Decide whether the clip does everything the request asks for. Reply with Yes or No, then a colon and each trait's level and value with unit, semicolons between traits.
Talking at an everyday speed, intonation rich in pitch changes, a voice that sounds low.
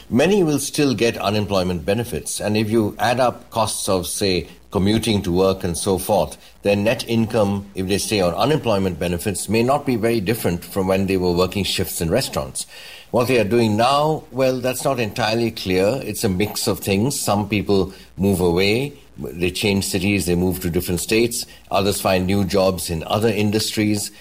No: average, 190 wpm; average, 3.4 semitones; low, 100 Hz